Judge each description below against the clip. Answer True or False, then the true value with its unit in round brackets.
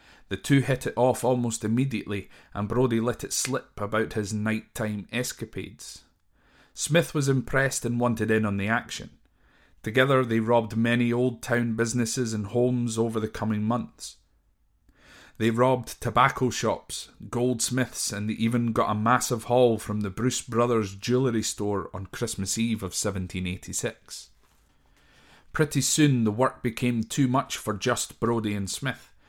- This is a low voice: True (115 Hz)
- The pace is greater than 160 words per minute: False (150 wpm)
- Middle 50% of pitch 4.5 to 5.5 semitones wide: False (3.0 semitones)